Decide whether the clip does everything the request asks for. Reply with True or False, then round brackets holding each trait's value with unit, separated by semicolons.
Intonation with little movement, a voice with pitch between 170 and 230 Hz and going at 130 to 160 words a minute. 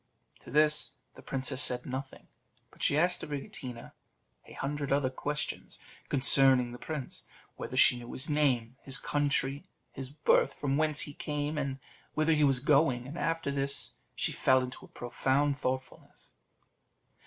False (2.2 semitones; 140 Hz; 155 wpm)